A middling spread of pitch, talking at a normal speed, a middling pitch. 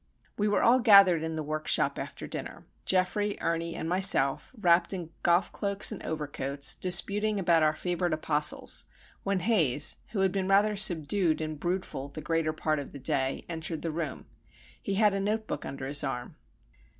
Yes: average, 4.3 semitones; average, 175 wpm; medium, 170 Hz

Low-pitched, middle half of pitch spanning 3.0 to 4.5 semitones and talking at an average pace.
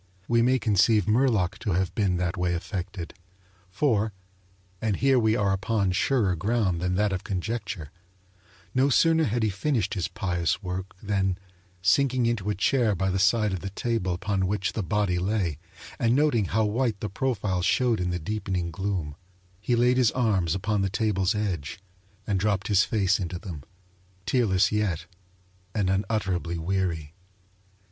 Yes: low, 100 Hz; average, 3.4 semitones; average, 165 wpm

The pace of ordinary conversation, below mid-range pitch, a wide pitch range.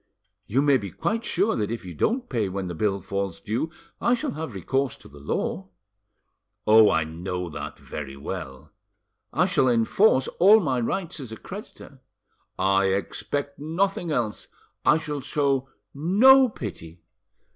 Yes: average, 155 wpm; low, 125 Hz; wide, 8.7 semitones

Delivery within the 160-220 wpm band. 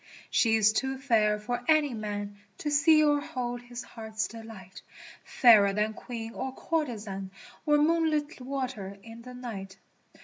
Yes: average, 165 wpm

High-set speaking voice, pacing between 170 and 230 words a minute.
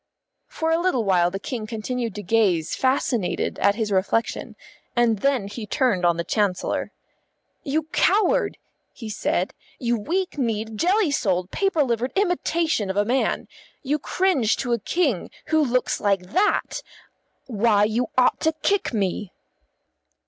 No: high, 235 Hz; average, 150 wpm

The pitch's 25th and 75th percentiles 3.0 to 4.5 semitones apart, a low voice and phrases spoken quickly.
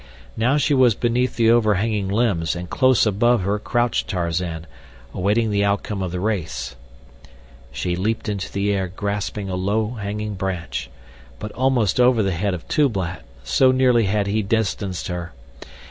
No: average, 3.7 semitones; low, 100 Hz; average, 160 wpm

